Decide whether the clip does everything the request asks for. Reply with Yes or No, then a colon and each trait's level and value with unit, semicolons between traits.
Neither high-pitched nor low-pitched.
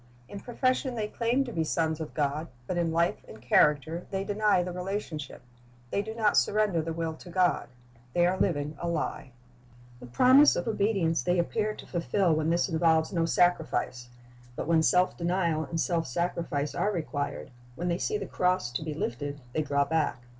Yes: medium, 170 Hz